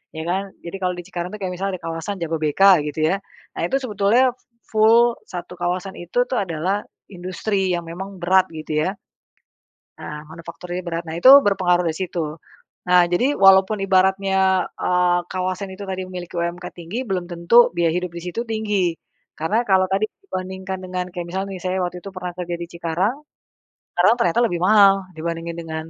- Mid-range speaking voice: Yes, medium, 180 Hz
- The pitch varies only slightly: Yes, narrow, 2.2 semitones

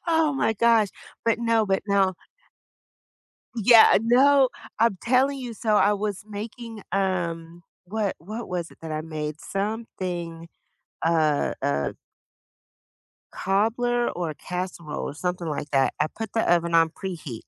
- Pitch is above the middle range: Yes, high, 195 Hz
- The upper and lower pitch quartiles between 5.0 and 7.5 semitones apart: Yes, wide, 5.4 semitones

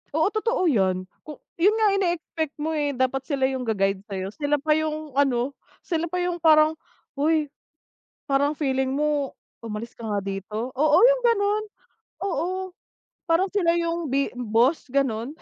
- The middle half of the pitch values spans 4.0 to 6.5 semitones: Yes, average, 4.7 semitones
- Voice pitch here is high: Yes, very high, 295 Hz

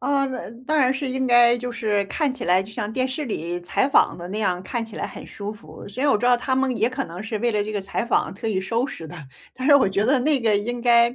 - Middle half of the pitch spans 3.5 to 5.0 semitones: Yes, average, 4.0 semitones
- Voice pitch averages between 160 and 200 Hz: No, high, 235 Hz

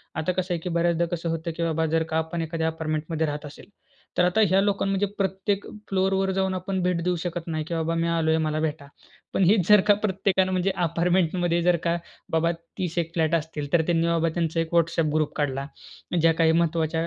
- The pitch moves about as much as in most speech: No, narrow, 2.2 semitones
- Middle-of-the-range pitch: Yes, medium, 170 Hz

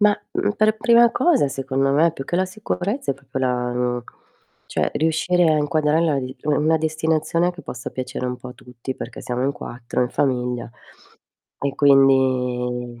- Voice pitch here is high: No, medium, 140 Hz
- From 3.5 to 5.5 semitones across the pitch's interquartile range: Yes, average, 4.4 semitones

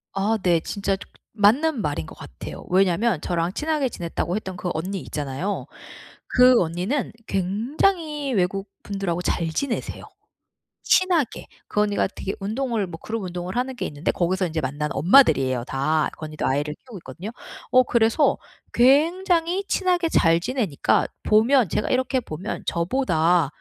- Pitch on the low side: No, high, 200 Hz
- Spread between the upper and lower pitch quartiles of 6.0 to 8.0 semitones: Yes, wide, 7.1 semitones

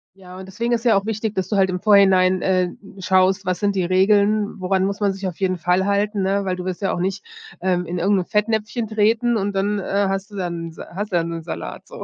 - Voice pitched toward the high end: Yes, high, 195 Hz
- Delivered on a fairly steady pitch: Yes, narrow, 2.0 semitones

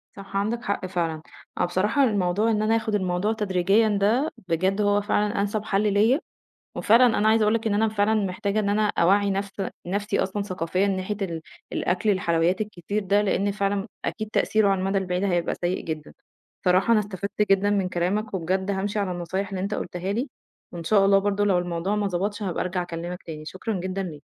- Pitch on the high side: Yes, high, 200 Hz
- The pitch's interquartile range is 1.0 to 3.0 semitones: Yes, narrow, 2.4 semitones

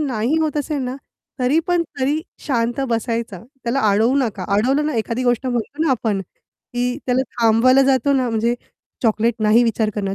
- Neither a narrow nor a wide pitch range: Yes, average, 3.2 semitones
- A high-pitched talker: Yes, high, 245 Hz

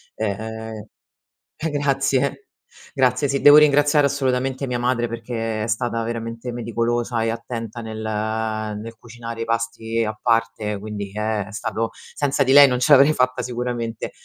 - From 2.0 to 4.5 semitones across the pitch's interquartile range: Yes, narrow, 2.4 semitones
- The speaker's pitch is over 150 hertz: No, low, 115 Hz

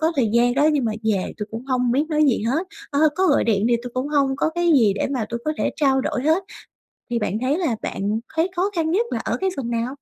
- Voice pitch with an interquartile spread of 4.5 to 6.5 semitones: Yes, average, 5.1 semitones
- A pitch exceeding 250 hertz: Yes, very high, 265 Hz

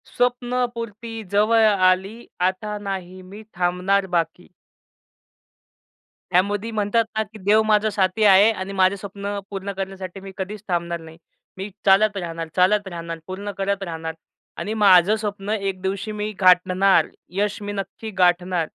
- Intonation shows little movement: Yes, narrow, 2.3 semitones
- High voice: Yes, high, 195 Hz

